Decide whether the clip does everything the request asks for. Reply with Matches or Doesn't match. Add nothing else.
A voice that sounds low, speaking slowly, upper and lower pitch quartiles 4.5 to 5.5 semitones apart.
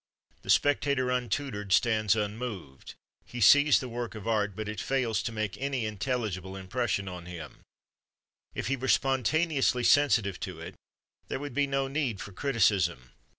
Doesn't match